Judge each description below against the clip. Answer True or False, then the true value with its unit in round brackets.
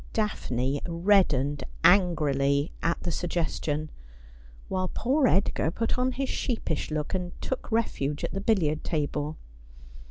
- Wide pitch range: True (5.7 semitones)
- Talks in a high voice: False (170 Hz)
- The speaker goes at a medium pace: False (125 wpm)